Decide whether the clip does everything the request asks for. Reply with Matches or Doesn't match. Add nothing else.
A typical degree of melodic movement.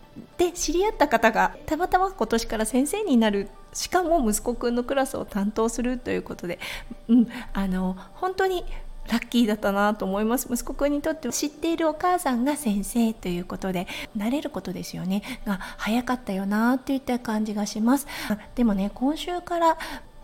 Doesn't match